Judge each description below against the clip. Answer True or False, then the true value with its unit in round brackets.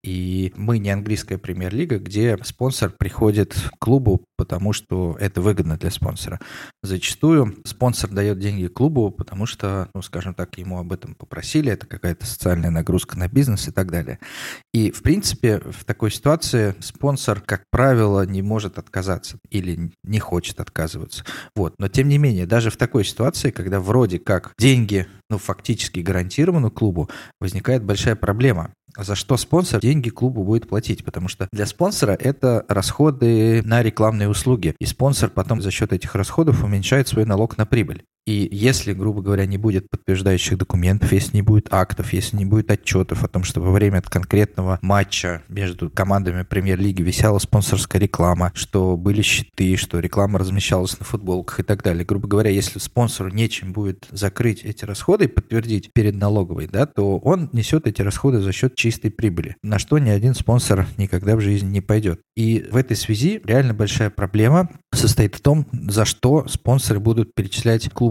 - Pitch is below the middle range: True (105 Hz)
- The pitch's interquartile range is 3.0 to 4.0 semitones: True (3.5 semitones)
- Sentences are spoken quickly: True (170 wpm)